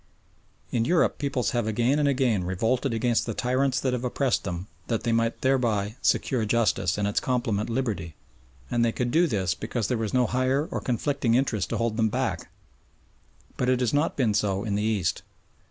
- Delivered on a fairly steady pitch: No, average, 3.3 semitones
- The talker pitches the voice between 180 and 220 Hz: No, low, 115 Hz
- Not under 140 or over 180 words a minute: No, average, 195 wpm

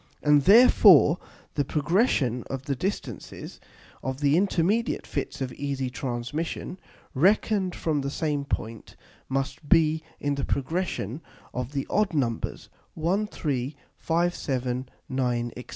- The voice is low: No, medium, 145 Hz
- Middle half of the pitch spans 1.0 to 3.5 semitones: No, average, 4.7 semitones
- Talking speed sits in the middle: No, slow, 130 wpm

